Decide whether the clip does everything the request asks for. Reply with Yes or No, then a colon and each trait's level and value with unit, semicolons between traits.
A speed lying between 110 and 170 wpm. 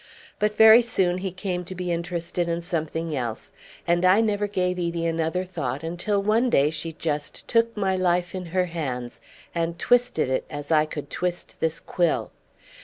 No: average, 180 wpm